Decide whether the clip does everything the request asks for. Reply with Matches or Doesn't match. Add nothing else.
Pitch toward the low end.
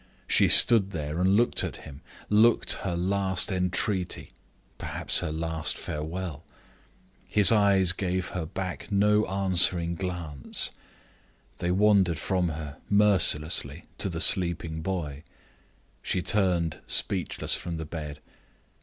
Matches